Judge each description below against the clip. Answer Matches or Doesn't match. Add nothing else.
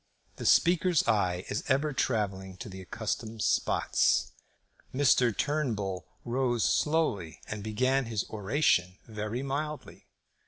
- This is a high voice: Doesn't match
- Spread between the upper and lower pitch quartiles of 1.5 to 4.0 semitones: Doesn't match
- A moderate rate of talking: Doesn't match